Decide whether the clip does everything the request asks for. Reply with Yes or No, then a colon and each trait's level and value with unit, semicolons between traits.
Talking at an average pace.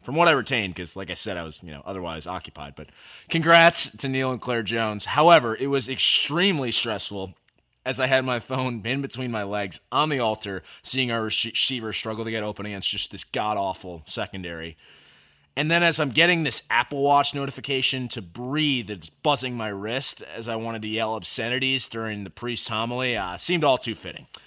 Yes: average, 195 wpm